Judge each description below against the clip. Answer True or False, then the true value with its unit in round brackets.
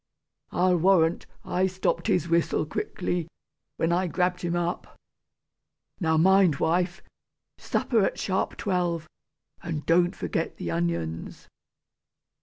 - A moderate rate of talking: False (115 wpm)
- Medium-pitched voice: True (175 Hz)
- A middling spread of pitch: False (2.3 semitones)